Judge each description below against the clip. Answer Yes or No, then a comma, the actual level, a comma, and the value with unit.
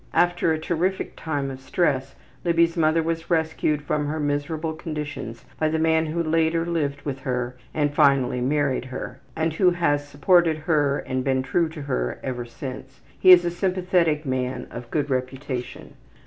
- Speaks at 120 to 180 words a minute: Yes, average, 170 wpm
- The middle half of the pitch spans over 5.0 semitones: No, average, 3.5 semitones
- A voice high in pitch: No, medium, 150 Hz